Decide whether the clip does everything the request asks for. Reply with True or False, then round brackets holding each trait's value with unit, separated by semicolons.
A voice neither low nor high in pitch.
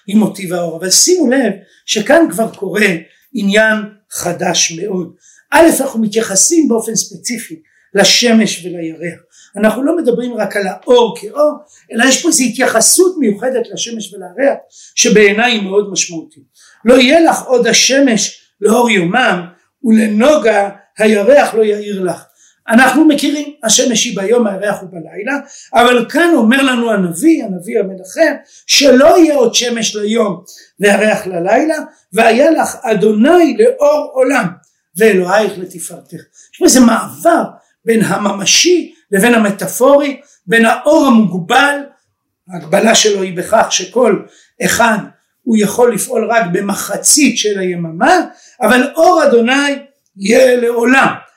False (225 Hz)